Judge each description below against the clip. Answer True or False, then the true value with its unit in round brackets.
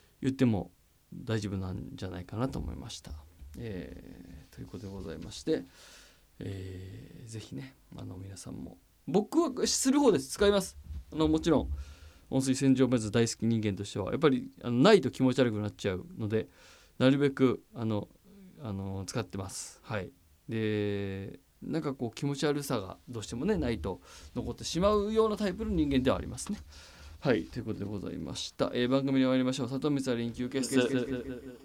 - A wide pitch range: True (5.7 semitones)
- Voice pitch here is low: True (120 Hz)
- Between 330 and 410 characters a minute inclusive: True (360 characters per minute)